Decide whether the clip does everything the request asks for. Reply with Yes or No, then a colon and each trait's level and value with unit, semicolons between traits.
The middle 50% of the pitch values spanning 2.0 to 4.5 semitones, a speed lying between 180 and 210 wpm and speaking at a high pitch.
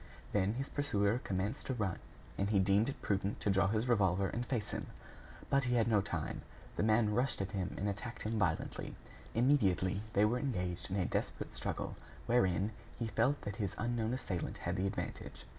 No: average, 3.6 semitones; average, 195 wpm; low, 105 Hz